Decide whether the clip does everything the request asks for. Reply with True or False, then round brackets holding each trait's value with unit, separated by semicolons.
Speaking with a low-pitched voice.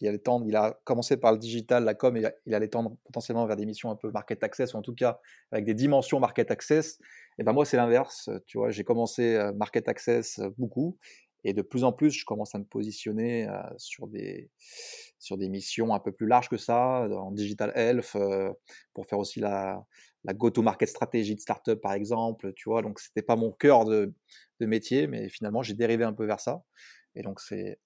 True (115 Hz)